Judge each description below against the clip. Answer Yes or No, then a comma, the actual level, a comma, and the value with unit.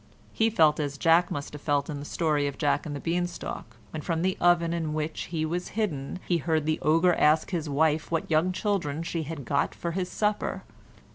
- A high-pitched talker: No, medium, 160 Hz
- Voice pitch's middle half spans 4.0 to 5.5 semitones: No, average, 2.8 semitones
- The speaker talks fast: Yes, fast, 220 wpm